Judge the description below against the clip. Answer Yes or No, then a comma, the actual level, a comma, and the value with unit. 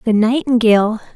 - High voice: Yes, high, 225 Hz